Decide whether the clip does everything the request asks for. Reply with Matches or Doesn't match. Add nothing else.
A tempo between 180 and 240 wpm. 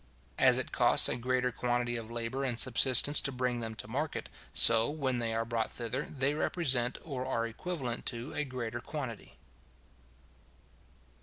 Doesn't match